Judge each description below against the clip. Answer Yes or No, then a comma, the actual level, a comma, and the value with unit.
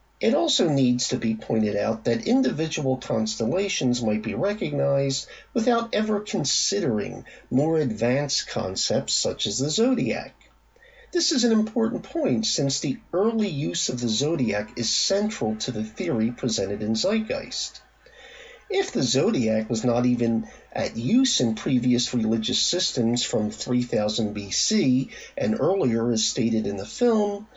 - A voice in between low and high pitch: No, low, 130 Hz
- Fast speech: No, average, 140 wpm